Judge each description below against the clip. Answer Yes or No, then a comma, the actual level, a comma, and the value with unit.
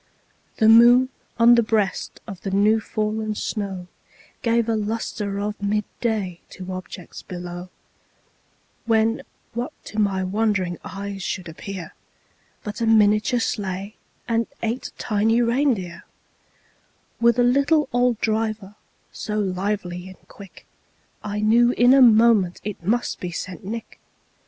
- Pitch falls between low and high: No, high, 215 Hz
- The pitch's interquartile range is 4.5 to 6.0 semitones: No, average, 3.1 semitones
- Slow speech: Yes, slow, 130 wpm